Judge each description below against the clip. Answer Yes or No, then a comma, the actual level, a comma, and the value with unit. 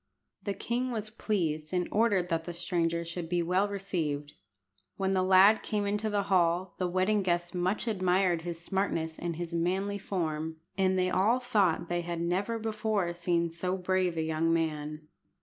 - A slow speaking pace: No, average, 175 wpm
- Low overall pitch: No, medium, 180 Hz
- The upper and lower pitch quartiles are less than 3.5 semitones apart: Yes, average, 2.9 semitones